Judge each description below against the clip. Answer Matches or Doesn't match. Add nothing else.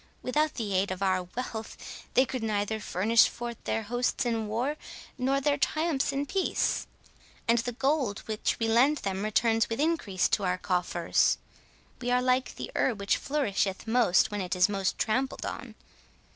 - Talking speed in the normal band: Matches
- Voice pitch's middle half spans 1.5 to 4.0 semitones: Doesn't match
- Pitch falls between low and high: Doesn't match